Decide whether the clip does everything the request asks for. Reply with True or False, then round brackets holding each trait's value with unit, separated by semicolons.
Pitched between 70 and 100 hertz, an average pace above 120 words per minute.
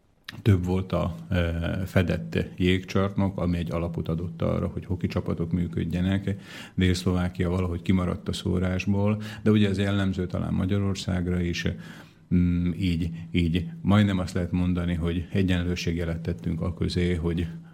True (90 Hz; 130 wpm)